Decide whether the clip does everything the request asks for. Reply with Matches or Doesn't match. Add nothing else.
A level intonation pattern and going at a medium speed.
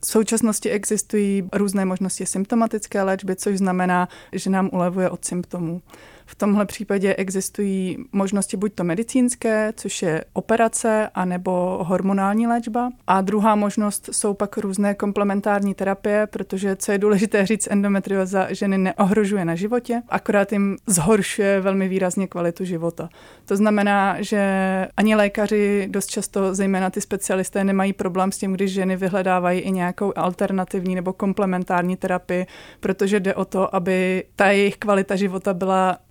Matches